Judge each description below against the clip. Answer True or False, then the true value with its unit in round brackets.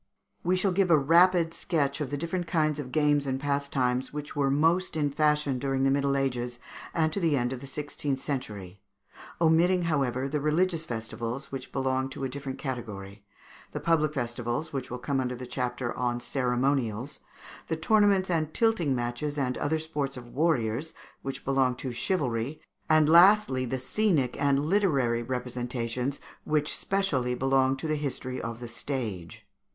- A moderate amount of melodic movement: True (3.9 semitones)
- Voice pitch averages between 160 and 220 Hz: False (140 Hz)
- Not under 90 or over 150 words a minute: False (165 wpm)